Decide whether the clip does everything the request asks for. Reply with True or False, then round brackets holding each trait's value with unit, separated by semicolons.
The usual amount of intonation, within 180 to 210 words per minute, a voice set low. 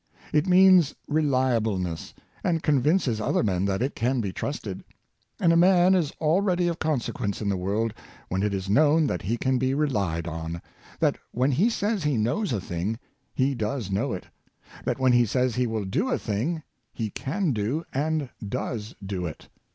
False (7.2 semitones; 190 wpm; 125 Hz)